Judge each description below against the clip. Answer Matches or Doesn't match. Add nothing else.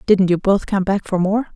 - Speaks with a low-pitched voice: Doesn't match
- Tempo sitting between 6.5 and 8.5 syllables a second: Doesn't match